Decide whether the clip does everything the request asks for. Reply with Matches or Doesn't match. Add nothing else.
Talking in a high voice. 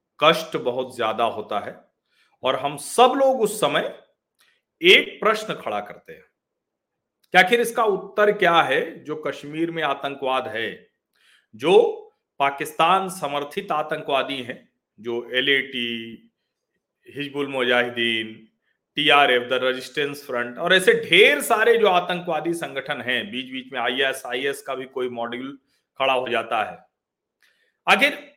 Doesn't match